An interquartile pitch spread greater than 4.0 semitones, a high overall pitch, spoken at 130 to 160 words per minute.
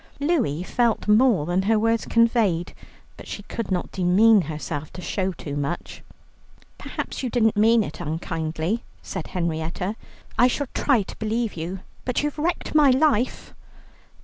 Yes: wide, 5.5 semitones; high, 210 Hz; average, 150 wpm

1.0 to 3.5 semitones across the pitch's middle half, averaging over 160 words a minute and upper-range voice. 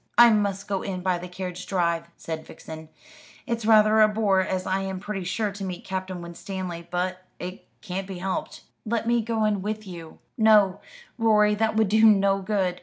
Yes: average, 2.8 semitones; average, 190 wpm; high, 195 Hz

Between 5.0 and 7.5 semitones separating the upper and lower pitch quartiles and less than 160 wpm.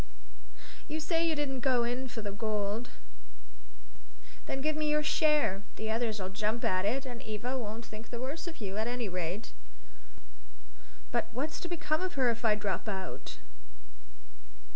No: wide, 5.6 semitones; average, 165 wpm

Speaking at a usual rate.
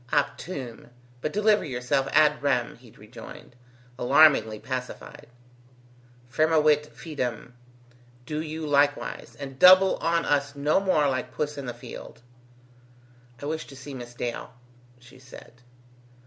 No: slow, 125 wpm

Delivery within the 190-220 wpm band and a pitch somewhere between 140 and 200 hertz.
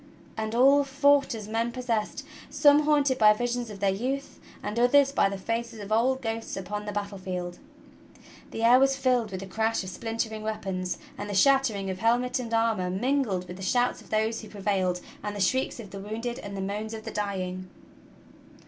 No: average, 200 wpm; high, 220 Hz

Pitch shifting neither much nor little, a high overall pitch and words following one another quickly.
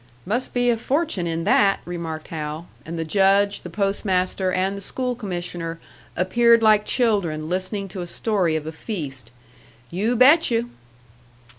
No: average, 5.0 semitones; high, 195 Hz; average, 160 wpm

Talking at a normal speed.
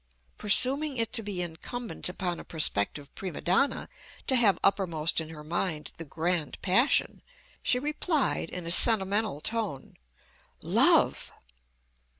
No: slow, 130 wpm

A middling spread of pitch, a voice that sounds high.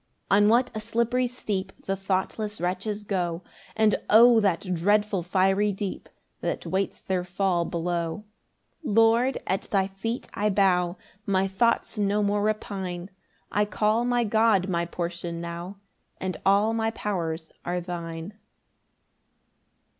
Yes: average, 3.1 semitones; high, 195 Hz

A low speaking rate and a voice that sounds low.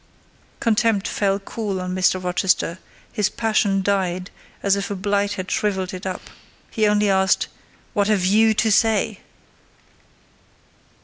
No: slow, 125 wpm; high, 200 Hz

